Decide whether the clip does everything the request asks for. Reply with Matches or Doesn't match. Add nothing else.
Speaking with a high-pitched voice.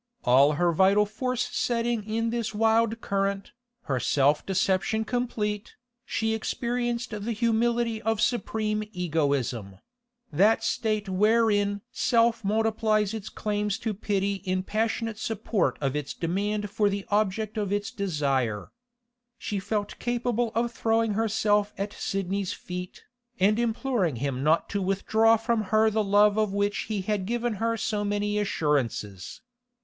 Matches